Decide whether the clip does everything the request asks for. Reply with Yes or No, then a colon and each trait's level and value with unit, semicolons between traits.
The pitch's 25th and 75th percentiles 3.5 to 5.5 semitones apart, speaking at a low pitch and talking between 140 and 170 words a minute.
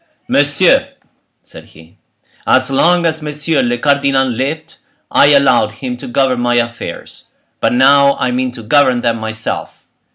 No: average, 2.7 semitones; low, 130 Hz; average, 150 wpm